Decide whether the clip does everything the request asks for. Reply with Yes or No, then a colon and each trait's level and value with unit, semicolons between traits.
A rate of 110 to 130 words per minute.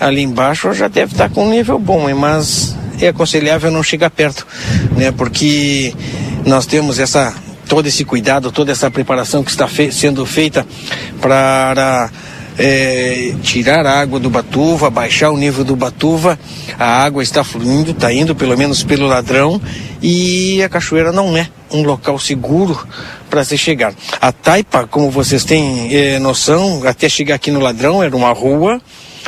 No: average, 160 wpm